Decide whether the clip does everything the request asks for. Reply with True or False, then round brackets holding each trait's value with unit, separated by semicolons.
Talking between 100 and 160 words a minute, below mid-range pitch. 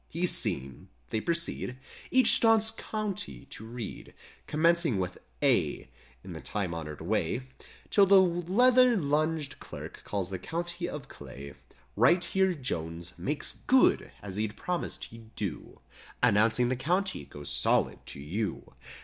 True (140 wpm; 130 Hz)